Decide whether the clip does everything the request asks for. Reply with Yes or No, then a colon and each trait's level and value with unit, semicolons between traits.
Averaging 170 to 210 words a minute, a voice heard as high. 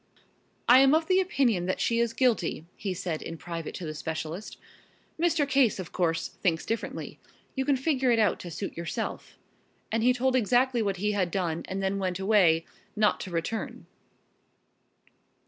Yes: average, 175 wpm; high, 205 Hz